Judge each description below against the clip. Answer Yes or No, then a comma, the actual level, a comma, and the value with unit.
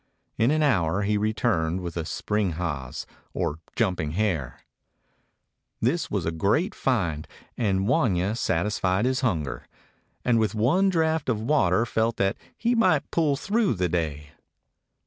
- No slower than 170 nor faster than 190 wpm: No, average, 145 wpm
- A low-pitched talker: Yes, low, 105 Hz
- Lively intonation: Yes, wide, 6.9 semitones